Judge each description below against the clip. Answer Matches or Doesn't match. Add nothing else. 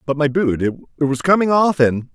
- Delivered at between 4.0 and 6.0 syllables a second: Matches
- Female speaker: Doesn't match